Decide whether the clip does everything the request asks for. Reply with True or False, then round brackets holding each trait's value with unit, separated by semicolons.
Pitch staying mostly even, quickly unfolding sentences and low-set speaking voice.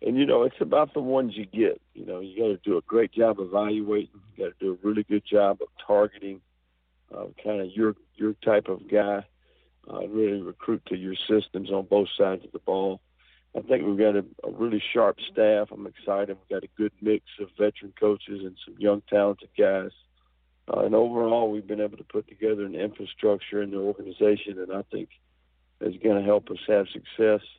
True (1.7 semitones; 215 wpm; 105 Hz)